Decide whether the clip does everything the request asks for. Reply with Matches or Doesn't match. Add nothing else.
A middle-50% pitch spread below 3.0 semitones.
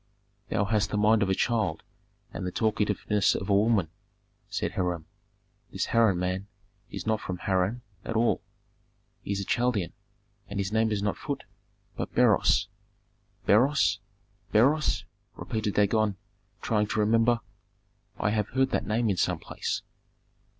Matches